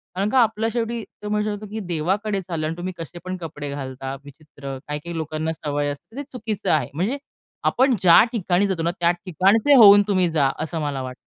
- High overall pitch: No, medium, 175 Hz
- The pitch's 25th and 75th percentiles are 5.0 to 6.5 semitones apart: Yes, average, 5.3 semitones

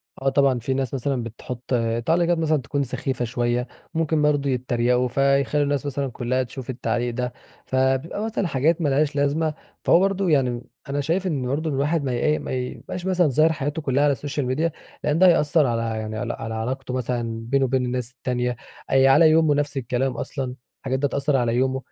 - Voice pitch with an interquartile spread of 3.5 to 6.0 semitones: No, average, 3.1 semitones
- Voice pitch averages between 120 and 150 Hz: Yes, low, 135 Hz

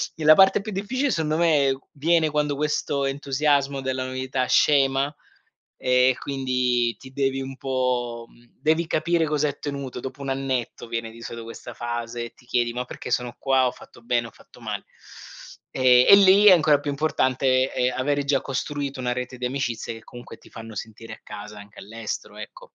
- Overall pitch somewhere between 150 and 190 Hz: No, low, 130 Hz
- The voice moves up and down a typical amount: Yes, average, 3.0 semitones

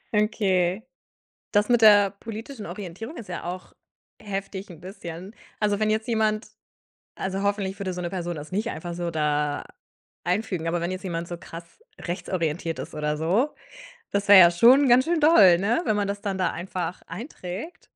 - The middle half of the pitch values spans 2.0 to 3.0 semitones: No, average, 3.7 semitones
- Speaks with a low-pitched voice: No, high, 190 Hz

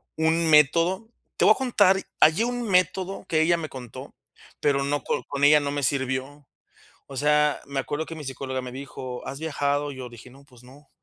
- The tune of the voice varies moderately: Yes, average, 3.4 semitones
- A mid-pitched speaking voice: Yes, medium, 145 Hz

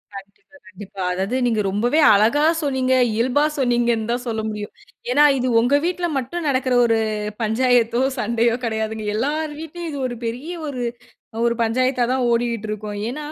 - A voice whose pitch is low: No, high, 240 Hz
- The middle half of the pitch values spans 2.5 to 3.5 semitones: Yes, average, 3.1 semitones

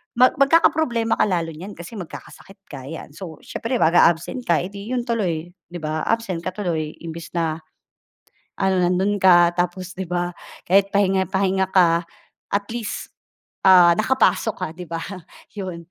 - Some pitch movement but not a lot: Yes, average, 3.1 semitones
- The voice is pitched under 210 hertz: Yes, medium, 185 Hz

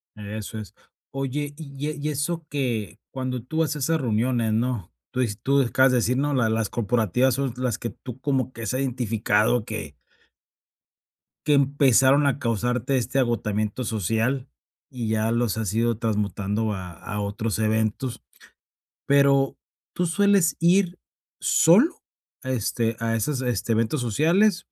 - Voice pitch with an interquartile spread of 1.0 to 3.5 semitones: No, average, 4.0 semitones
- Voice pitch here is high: No, low, 125 Hz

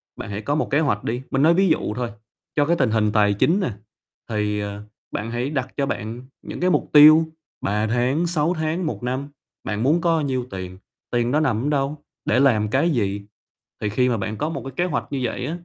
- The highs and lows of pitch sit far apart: Yes, wide, 6.1 semitones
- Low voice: Yes, low, 130 Hz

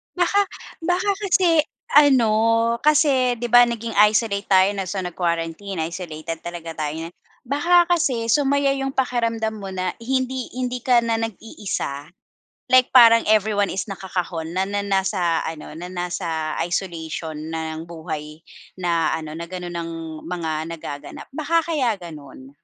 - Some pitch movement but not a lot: No, wide, 7.1 semitones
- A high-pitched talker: Yes, high, 195 Hz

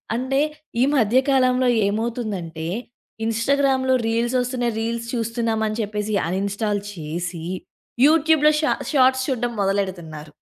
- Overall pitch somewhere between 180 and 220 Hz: No, high, 230 Hz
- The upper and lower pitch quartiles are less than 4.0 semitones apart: No, average, 4.3 semitones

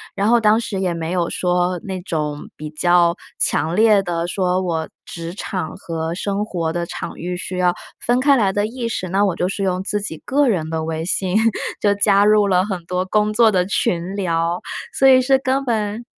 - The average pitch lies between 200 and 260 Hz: No, medium, 185 Hz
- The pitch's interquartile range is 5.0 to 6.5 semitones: No, average, 3.5 semitones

